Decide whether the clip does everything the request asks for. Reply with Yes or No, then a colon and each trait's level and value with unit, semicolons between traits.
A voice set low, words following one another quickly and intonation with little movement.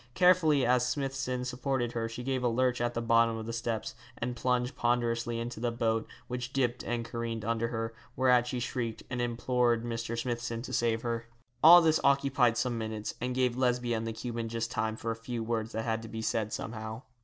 Yes: low, 120 Hz; fast, 210 wpm; narrow, 1.6 semitones